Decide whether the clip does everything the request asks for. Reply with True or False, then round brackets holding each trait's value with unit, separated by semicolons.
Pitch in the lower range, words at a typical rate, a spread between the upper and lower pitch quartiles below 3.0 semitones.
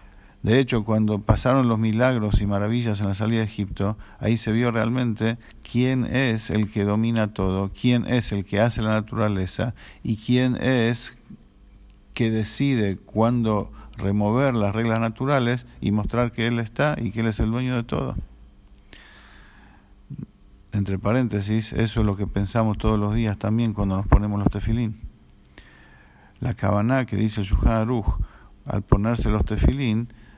True (110 Hz; 155 wpm; 2.5 semitones)